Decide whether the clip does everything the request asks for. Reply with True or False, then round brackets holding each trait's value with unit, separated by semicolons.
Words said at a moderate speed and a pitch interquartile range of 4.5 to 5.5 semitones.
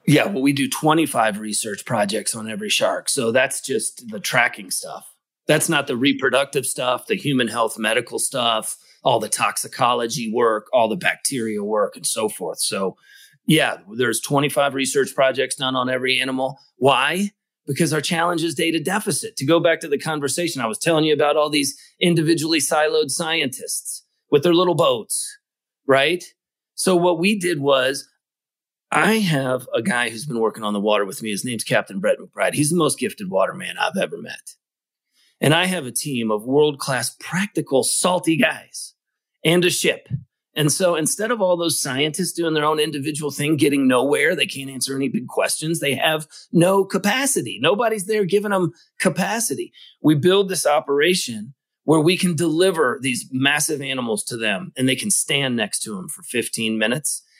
True (180 wpm; 5.1 semitones)